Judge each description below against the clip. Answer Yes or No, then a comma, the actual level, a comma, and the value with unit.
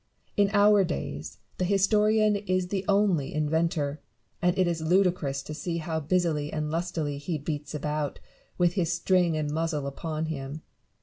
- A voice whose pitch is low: No, medium, 165 Hz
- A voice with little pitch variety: No, average, 3.5 semitones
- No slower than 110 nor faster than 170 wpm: Yes, average, 160 wpm